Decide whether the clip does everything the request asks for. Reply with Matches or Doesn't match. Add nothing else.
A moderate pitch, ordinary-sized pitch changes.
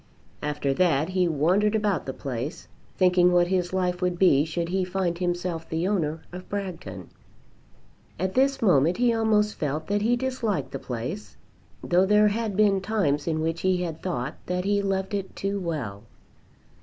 Matches